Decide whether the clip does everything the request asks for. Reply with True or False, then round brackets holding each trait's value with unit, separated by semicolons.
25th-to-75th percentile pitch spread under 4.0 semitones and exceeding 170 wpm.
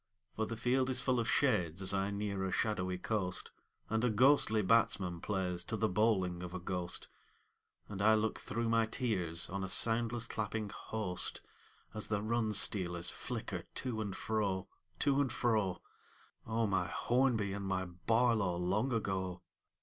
False (3.5 semitones; 165 wpm)